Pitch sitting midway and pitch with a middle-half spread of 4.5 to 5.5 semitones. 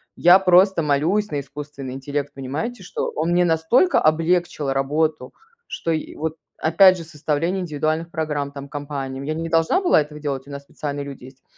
No: medium, 155 Hz; average, 3.0 semitones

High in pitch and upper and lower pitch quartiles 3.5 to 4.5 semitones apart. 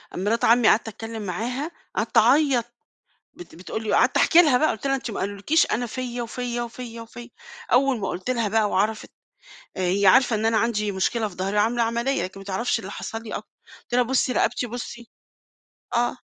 No: high, 230 Hz; average, 2.9 semitones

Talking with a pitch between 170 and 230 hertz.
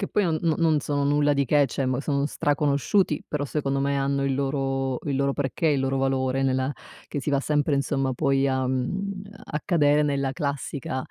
No: medium, 140 Hz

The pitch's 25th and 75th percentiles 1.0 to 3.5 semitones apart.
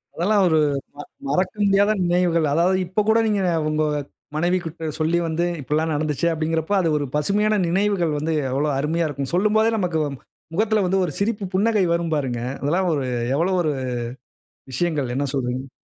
No: average, 4.1 semitones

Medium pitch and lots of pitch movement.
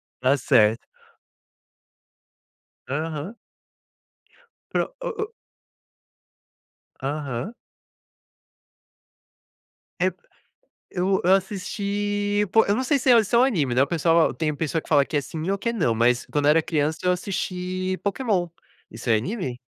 Yes: medium, 175 Hz; wide, 5.9 semitones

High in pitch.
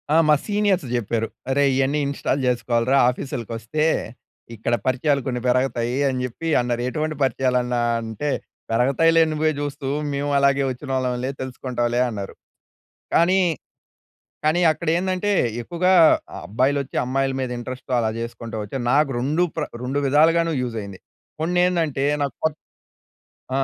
No: low, 135 Hz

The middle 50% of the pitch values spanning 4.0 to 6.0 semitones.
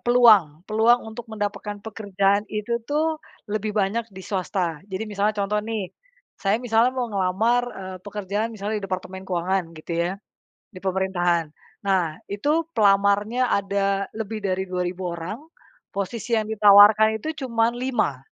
No: average, 2.7 semitones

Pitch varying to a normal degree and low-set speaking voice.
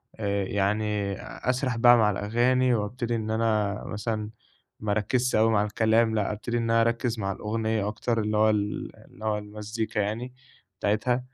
No: narrow, 1.9 semitones; low, 110 Hz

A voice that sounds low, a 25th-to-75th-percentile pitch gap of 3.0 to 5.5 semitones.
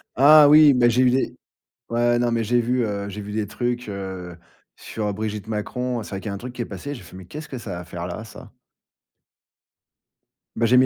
Yes: low, 115 Hz; average, 3.6 semitones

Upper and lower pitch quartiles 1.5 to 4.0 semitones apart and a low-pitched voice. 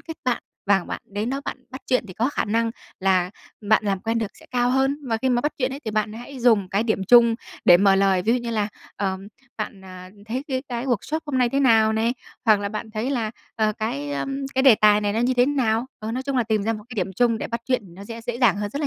No: average, 3.3 semitones; high, 225 Hz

